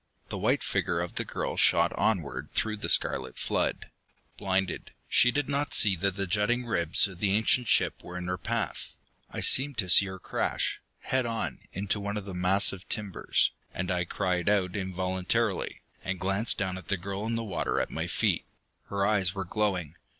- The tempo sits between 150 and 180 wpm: No, average, 190 wpm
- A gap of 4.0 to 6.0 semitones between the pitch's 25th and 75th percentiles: No, average, 2.8 semitones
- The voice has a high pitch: No, very low, 95 Hz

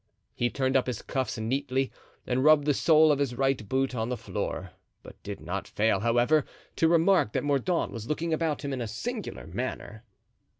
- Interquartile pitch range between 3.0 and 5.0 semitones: Yes, average, 4.0 semitones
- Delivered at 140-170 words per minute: No, average, 195 wpm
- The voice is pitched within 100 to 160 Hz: Yes, low, 135 Hz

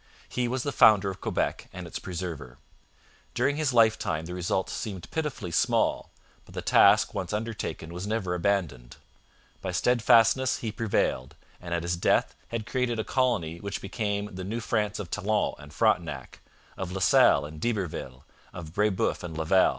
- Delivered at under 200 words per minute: Yes, average, 165 wpm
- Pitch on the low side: Yes, very low, 95 Hz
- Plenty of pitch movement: No, average, 4.7 semitones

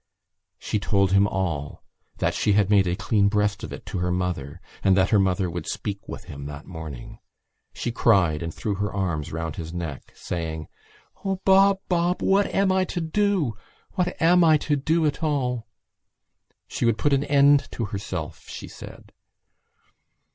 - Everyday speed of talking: Yes, average, 175 wpm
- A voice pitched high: No, low, 100 Hz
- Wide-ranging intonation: Yes, wide, 9.0 semitones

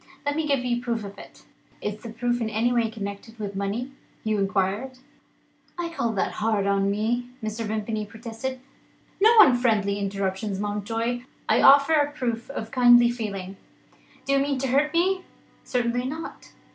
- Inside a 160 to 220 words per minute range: Yes, average, 170 wpm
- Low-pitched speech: No, high, 230 Hz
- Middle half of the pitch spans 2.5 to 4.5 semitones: Yes, average, 3.8 semitones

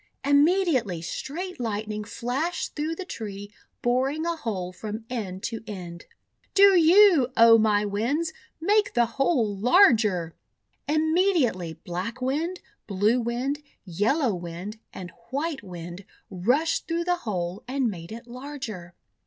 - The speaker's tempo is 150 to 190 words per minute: No, slow, 135 wpm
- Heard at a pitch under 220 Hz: No, high, 235 Hz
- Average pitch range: No, wide, 7.4 semitones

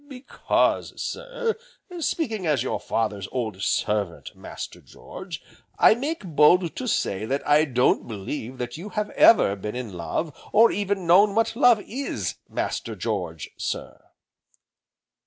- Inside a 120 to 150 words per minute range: Yes, average, 140 wpm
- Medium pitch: Yes, medium, 150 Hz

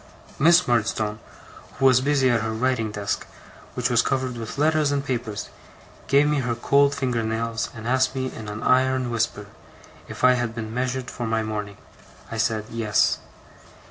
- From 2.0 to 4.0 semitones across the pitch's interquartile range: Yes, average, 2.8 semitones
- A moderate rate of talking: Yes, average, 175 wpm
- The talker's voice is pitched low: Yes, low, 120 Hz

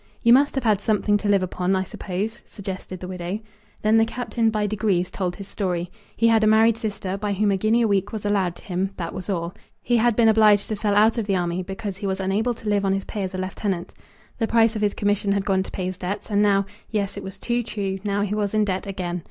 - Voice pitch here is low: No, high, 200 Hz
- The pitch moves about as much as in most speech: No, narrow, 2.3 semitones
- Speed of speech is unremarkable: No, fast, 265 wpm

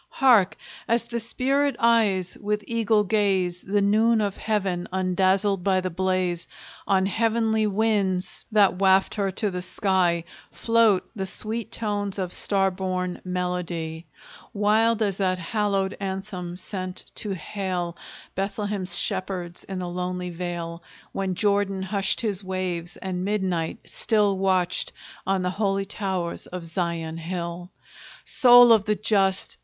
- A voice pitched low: No, high, 190 Hz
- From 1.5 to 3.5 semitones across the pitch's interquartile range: Yes, narrow, 2.5 semitones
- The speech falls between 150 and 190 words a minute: No, slow, 135 wpm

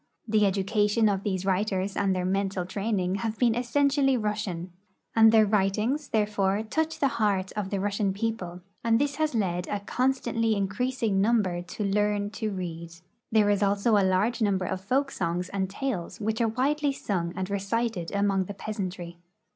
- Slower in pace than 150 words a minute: No, average, 170 wpm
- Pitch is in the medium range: No, high, 205 Hz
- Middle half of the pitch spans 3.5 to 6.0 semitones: No, average, 3.0 semitones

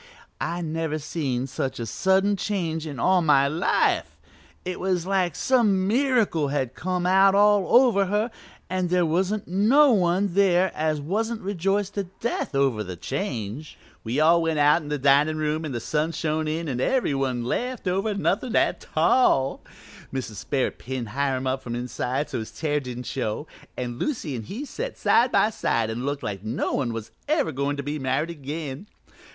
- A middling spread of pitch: No, wide, 6.4 semitones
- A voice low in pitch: No, medium, 160 Hz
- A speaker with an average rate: Yes, average, 185 wpm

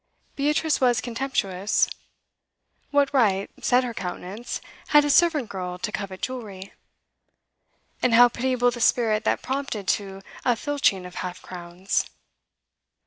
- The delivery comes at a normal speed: No, slow, 130 wpm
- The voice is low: No, high, 230 Hz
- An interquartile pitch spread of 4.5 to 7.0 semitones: Yes, average, 5.3 semitones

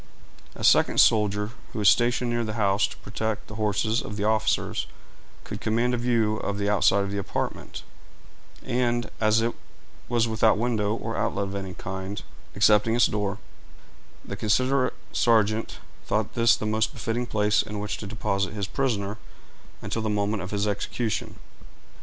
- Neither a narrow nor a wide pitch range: No, narrow, 2.0 semitones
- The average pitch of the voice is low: Yes, low, 110 Hz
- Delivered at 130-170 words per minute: Yes, average, 165 wpm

